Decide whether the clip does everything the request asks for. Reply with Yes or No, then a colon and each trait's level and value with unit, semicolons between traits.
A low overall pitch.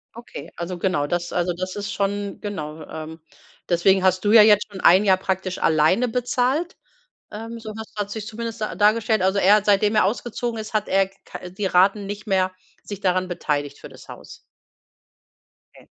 No: high, 200 Hz